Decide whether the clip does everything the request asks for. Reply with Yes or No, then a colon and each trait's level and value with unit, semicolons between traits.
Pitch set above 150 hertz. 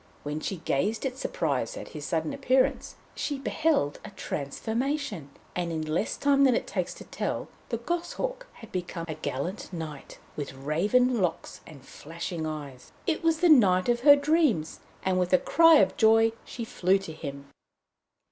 Yes: high, 190 Hz